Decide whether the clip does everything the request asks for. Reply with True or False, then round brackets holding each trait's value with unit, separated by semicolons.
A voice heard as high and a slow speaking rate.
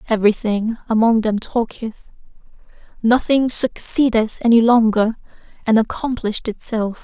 True (225 Hz; 95 wpm)